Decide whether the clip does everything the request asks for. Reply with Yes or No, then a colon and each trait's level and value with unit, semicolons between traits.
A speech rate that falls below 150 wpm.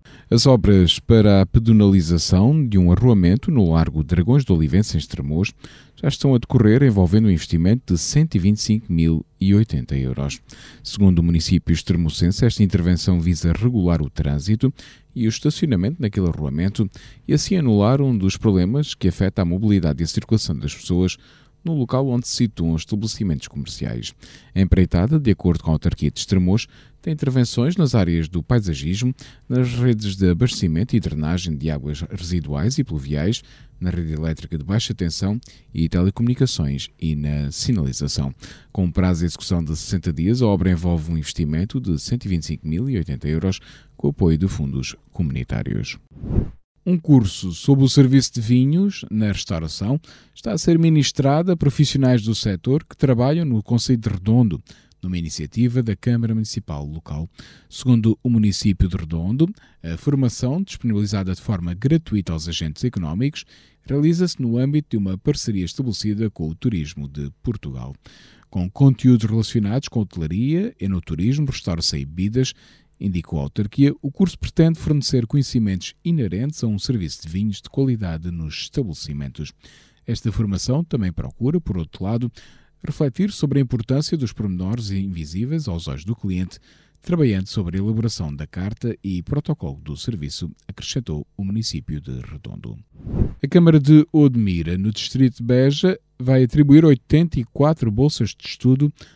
No: average, 155 wpm